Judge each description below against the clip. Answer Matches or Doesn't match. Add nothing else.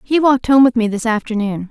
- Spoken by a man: Doesn't match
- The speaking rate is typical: Doesn't match